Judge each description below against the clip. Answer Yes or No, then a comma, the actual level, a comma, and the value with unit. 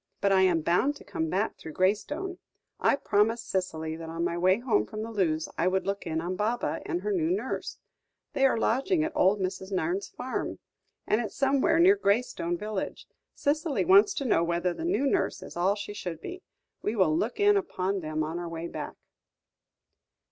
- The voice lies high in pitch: Yes, high, 200 Hz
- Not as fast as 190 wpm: No, average, 195 wpm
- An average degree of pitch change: No, wide, 7.9 semitones